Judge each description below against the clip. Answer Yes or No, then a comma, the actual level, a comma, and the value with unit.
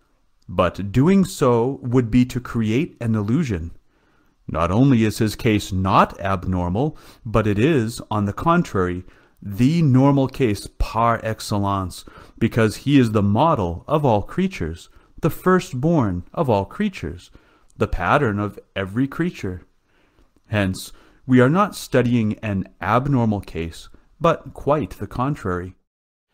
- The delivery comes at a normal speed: No, slow, 130 wpm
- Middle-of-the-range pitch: No, low, 110 Hz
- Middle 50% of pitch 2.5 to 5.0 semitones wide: No, wide, 5.5 semitones